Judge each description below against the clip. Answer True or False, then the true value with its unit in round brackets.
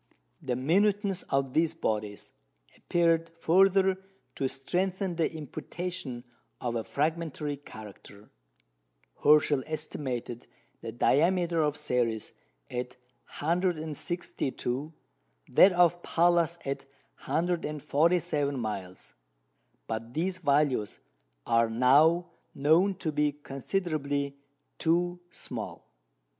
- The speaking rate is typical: False (90 wpm)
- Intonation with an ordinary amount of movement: True (4.8 semitones)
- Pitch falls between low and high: True (150 Hz)